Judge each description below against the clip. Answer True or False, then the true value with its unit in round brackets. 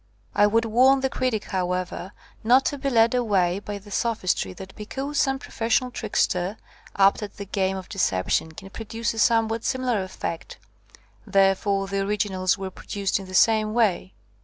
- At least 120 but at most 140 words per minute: False (175 wpm)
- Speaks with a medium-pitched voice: False (205 Hz)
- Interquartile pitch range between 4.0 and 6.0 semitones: False (3.3 semitones)